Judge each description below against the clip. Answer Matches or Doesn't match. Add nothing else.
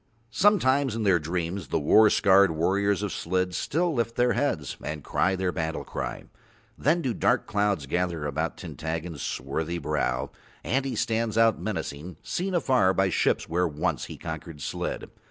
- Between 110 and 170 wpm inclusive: Matches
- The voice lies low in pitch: Matches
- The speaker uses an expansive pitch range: Matches